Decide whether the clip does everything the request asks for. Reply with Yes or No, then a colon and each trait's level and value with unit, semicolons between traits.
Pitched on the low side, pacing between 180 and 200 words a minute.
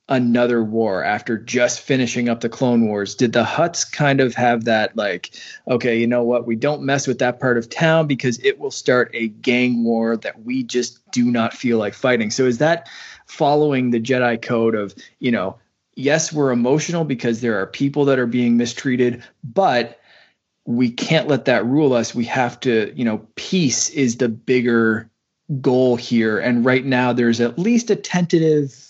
Yes: low, 125 Hz; average, 190 wpm